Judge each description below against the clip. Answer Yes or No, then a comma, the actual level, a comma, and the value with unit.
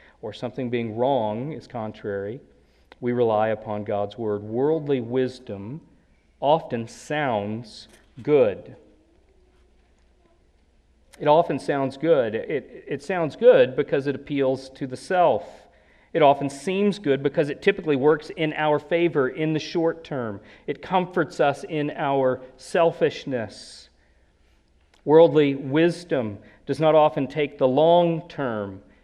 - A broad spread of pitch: Yes, wide, 6.5 semitones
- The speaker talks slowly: Yes, slow, 125 wpm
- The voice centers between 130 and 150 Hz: Yes, low, 135 Hz